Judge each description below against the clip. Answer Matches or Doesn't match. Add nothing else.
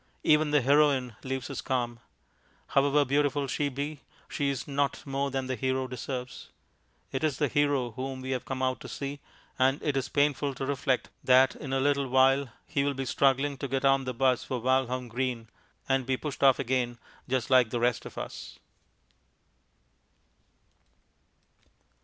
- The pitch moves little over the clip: Matches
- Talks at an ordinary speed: Matches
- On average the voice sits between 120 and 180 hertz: Matches